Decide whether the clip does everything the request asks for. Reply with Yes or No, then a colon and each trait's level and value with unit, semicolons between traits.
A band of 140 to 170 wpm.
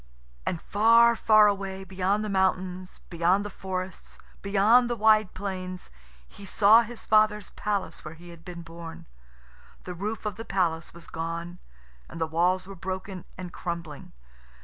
Yes: average, 155 wpm